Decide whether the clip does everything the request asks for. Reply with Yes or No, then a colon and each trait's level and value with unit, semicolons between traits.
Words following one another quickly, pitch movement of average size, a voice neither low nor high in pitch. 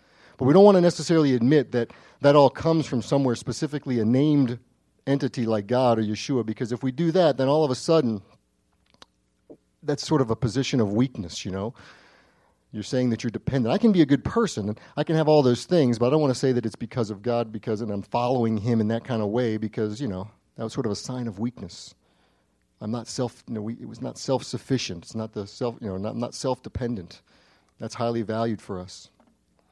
No: fast, 230 wpm; average, 3.8 semitones; low, 120 Hz